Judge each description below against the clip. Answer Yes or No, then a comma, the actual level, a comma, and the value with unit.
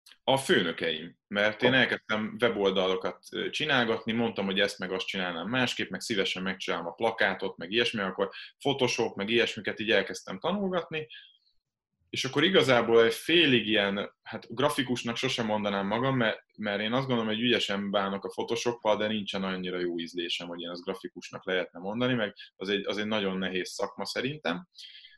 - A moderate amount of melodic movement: Yes, average, 3.6 semitones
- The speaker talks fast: Yes, fast, 160 wpm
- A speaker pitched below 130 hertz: Yes, low, 110 Hz